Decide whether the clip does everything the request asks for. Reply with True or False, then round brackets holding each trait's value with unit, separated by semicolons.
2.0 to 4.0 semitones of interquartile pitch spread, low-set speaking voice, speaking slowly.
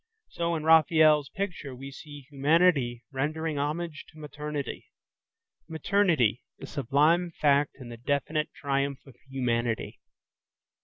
False (2.8 semitones; 145 Hz; 110 wpm)